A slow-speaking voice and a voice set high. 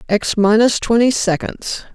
Yes: slow, 125 wpm; high, 220 Hz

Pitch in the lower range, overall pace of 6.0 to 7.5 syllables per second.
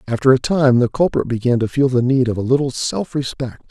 No: low, 130 Hz; 5.7 syllables/s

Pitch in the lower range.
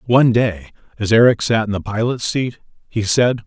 Yes: low, 110 Hz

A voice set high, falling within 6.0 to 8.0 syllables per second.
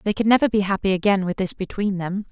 Yes: high, 195 Hz; 6.5 syllables/s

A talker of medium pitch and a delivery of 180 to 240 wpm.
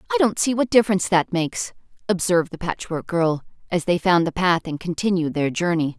Yes: medium, 180 Hz; average, 200 wpm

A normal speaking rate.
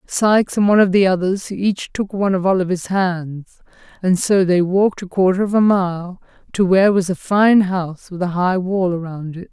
No: fast, 210 wpm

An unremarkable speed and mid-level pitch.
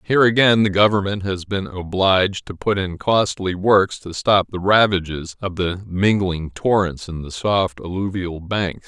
No: average, 170 wpm; very low, 95 Hz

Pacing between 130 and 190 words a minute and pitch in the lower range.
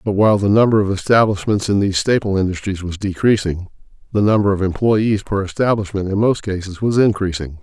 Yes: average, 180 wpm; low, 100 Hz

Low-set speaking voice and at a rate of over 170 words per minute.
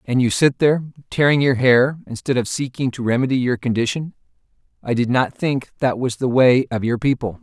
Yes: low, 130 Hz; average, 200 wpm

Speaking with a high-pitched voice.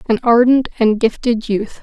Yes: high, 230 Hz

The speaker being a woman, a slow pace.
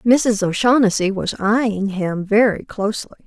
Yes: female; slow, 130 wpm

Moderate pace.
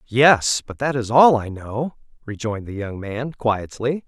Yes: average, 175 wpm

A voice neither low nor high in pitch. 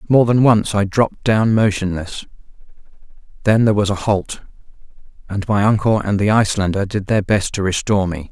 No: low, 105 Hz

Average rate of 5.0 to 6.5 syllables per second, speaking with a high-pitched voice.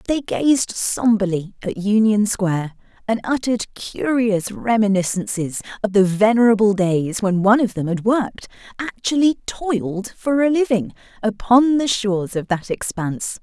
No: 4.6 syllables/s; high, 215 Hz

